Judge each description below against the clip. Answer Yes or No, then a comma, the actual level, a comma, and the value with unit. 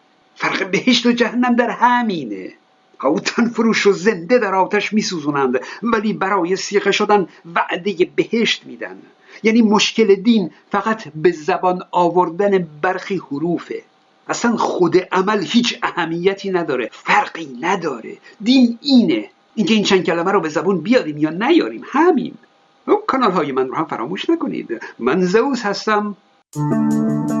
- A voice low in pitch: No, high, 205 Hz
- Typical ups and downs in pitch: Yes, average, 4.7 semitones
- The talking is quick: No, average, 135 wpm